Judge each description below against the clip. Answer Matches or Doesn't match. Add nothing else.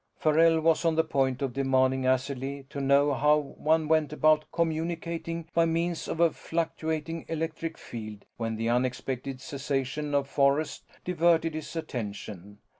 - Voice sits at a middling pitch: Matches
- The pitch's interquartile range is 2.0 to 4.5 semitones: Matches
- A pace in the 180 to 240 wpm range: Doesn't match